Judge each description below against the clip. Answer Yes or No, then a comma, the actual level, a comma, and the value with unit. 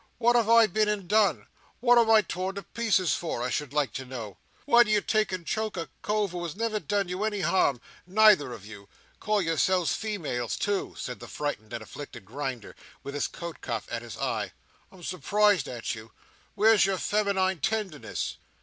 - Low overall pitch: No, medium, 185 Hz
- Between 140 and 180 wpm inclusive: No, fast, 205 wpm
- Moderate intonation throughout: No, wide, 7.3 semitones